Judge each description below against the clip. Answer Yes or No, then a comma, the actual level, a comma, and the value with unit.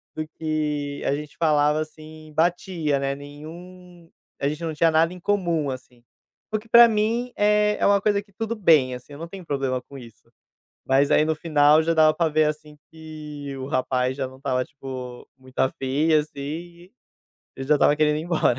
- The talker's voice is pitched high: No, medium, 155 Hz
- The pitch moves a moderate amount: Yes, average, 3.3 semitones